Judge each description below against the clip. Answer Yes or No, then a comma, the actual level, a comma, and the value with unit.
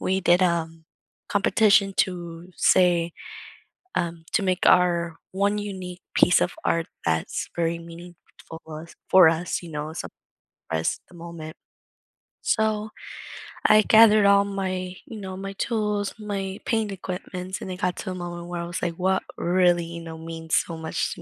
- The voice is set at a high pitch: No, medium, 180 Hz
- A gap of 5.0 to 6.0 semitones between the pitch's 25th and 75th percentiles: No, average, 2.7 semitones